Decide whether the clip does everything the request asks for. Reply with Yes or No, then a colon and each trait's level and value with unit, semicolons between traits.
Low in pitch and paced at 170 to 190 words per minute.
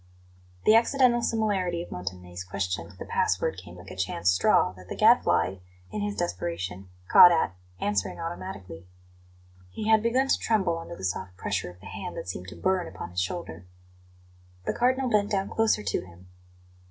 Yes: low, 100 Hz; average, 175 wpm